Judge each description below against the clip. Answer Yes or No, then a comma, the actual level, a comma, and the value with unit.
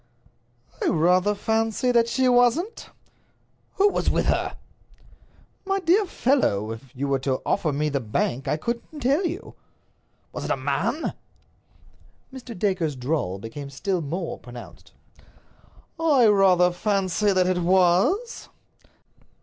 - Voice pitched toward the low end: No, high, 190 Hz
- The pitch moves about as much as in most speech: No, wide, 9.0 semitones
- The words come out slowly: Yes, slow, 130 wpm